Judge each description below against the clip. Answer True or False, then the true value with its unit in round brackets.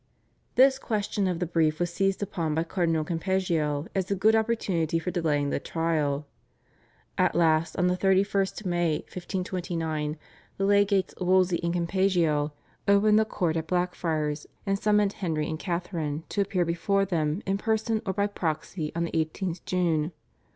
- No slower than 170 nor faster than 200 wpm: False (160 wpm)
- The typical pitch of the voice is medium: True (175 Hz)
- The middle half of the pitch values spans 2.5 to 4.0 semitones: True (3.4 semitones)